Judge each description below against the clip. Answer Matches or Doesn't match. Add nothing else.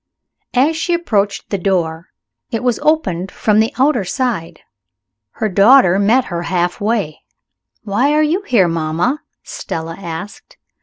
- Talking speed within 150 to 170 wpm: Doesn't match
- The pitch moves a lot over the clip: Matches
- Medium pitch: Doesn't match